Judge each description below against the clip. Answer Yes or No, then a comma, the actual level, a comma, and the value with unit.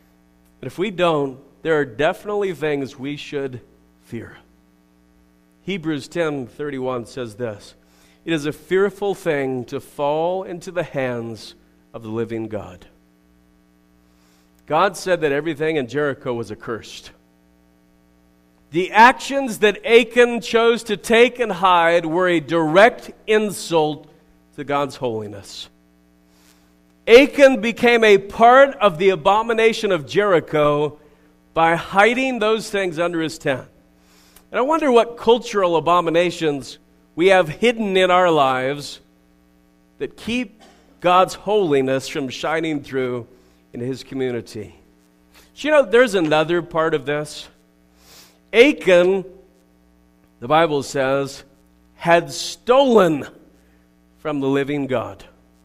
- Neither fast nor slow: No, slow, 120 wpm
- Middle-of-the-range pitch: Yes, medium, 145 Hz